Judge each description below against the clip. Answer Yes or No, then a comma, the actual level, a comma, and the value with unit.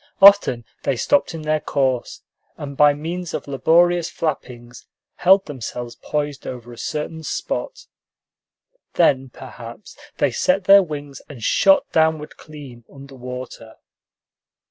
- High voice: No, medium, 145 Hz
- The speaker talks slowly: Yes, slow, 125 wpm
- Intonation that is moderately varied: Yes, average, 4.6 semitones